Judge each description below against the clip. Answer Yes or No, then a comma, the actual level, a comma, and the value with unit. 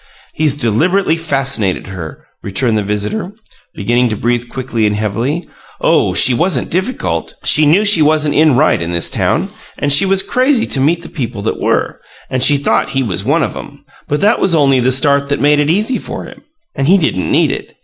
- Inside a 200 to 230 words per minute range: Yes, fast, 205 wpm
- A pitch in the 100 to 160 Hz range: Yes, medium, 140 Hz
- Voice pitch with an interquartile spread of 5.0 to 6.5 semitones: Yes, wide, 5.6 semitones